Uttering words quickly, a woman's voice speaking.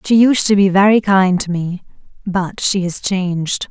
No: average, 195 wpm; female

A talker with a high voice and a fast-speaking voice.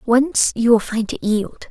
Yes: high, 235 Hz; fast, 210 wpm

